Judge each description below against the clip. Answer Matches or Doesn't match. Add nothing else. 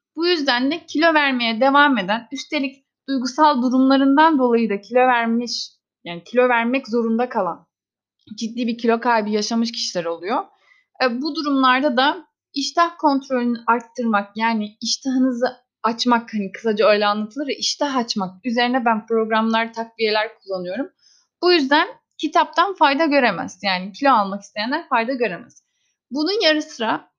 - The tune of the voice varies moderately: Matches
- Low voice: Doesn't match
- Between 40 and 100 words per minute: Doesn't match